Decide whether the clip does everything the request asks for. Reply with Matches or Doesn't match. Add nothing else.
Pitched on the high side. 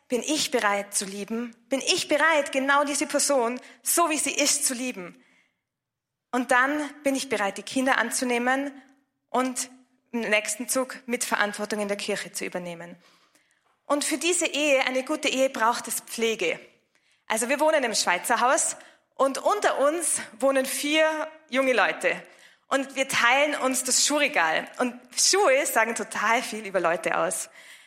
Matches